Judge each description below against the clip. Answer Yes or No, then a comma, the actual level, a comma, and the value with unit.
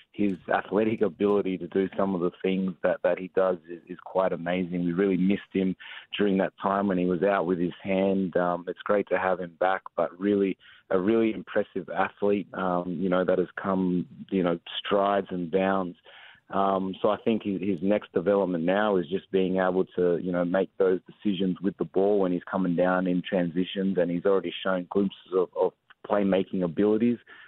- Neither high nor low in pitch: No, very low, 95 Hz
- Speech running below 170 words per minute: No, average, 200 wpm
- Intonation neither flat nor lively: No, narrow, 1.6 semitones